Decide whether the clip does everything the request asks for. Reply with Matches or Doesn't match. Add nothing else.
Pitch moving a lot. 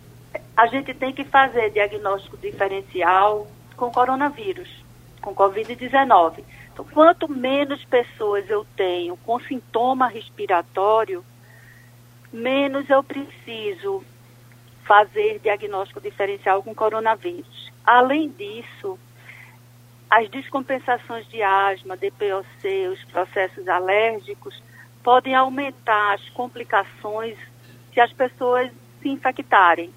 Matches